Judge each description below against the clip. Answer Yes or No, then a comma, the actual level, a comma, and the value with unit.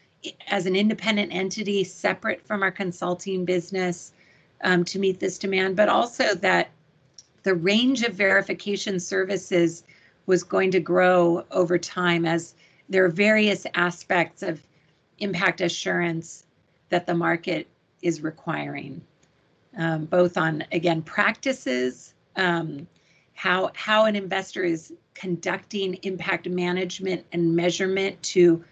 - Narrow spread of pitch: Yes, narrow, 2.1 semitones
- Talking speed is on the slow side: Yes, slow, 120 wpm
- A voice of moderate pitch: Yes, medium, 180 Hz